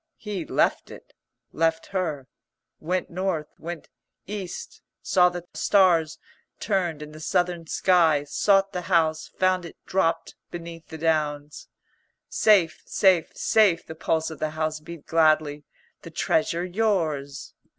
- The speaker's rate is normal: No, slow, 130 wpm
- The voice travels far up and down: No, average, 2.8 semitones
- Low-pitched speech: No, medium, 165 Hz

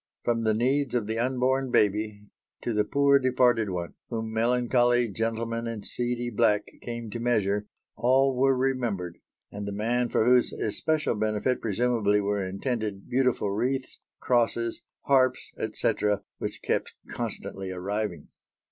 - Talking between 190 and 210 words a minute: No, average, 140 wpm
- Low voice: Yes, low, 115 Hz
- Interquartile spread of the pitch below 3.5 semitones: Yes, average, 3.1 semitones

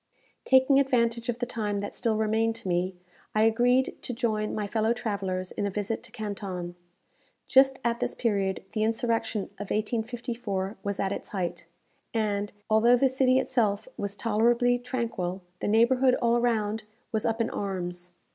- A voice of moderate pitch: No, high, 220 Hz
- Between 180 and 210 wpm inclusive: No, average, 165 wpm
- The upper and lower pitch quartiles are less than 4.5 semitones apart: Yes, average, 3.0 semitones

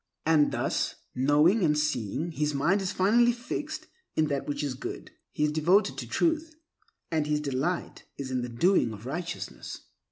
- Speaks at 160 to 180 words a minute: Yes, average, 170 wpm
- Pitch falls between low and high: Yes, medium, 150 Hz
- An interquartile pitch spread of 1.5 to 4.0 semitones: No, average, 5.1 semitones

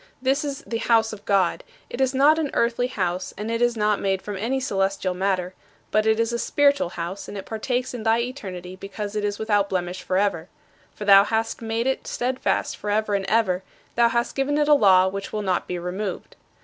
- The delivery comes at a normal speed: No, fast, 215 wpm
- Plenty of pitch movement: No, average, 3.7 semitones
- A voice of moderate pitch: No, high, 210 Hz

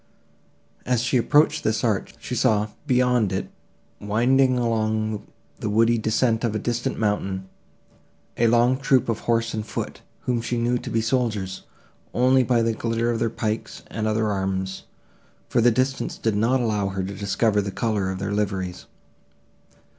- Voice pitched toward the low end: Yes, low, 115 Hz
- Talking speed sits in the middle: Yes, average, 165 wpm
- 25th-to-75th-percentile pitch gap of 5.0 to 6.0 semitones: No, average, 2.7 semitones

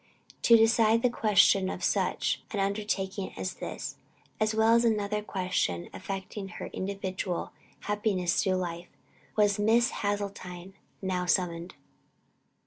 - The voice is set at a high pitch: Yes, high, 200 Hz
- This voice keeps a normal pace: No, slow, 125 wpm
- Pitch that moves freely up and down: No, average, 2.7 semitones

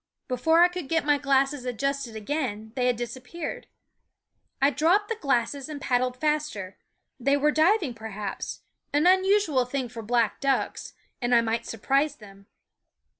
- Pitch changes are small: No, average, 4.2 semitones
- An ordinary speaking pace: Yes, average, 150 wpm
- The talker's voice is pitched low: No, very high, 270 Hz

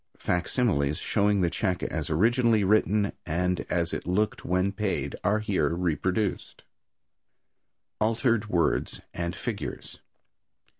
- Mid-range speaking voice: No, very low, 95 Hz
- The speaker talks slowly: Yes, slow, 110 wpm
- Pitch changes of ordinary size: Yes, average, 3.8 semitones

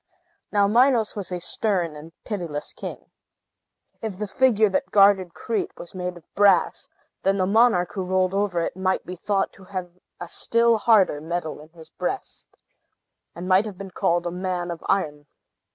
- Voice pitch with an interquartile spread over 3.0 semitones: No, average, 2.7 semitones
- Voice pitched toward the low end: No, medium, 185 Hz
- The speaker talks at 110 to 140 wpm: No, average, 175 wpm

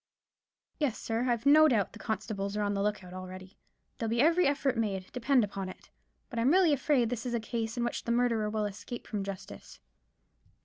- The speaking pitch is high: Yes, high, 225 Hz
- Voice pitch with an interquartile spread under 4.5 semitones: Yes, average, 3.6 semitones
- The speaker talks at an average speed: No, fast, 210 wpm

